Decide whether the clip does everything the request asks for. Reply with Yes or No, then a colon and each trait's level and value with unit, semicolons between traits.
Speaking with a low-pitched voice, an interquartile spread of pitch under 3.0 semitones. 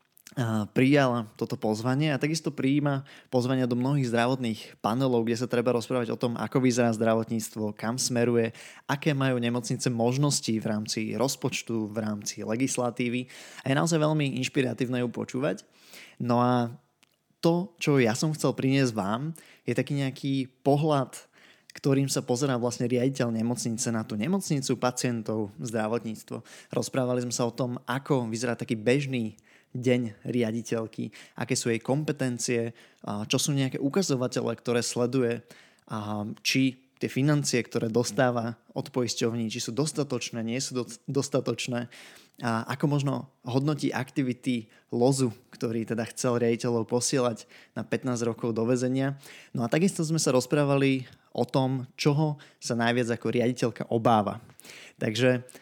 Yes: low, 125 Hz; narrow, 2.4 semitones